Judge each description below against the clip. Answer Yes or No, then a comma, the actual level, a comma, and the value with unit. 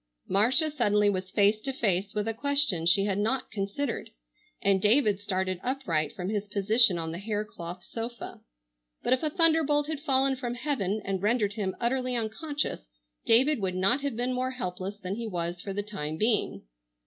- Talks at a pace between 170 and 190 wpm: Yes, average, 185 wpm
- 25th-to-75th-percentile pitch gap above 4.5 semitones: Yes, average, 5.0 semitones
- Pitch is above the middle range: Yes, high, 215 Hz